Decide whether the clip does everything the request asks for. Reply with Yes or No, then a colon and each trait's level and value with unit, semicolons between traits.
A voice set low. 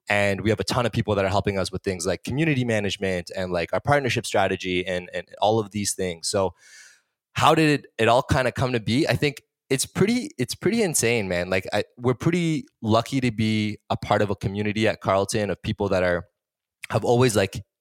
Yes: low, 110 Hz